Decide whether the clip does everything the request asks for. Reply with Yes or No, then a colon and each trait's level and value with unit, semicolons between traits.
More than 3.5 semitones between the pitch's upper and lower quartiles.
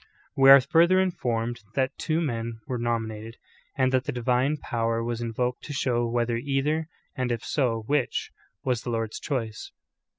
No: average, 2.9 semitones